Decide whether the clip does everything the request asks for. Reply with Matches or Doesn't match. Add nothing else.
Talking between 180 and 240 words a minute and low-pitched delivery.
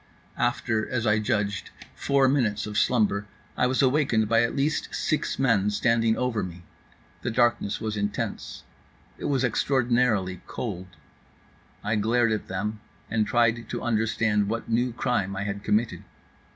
Doesn't match